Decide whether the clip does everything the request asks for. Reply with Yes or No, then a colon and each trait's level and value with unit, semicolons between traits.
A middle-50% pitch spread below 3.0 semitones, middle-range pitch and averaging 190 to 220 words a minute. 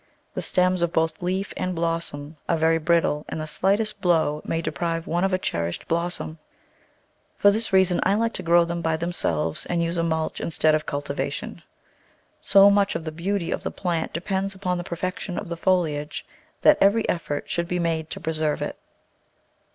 Yes: narrow, 2.6 semitones; medium, 170 Hz; average, 195 wpm